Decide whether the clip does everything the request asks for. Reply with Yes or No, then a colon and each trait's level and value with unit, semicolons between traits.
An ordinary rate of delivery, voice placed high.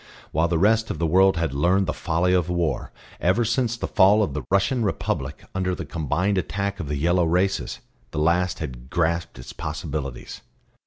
No: average, 190 wpm; very low, 90 Hz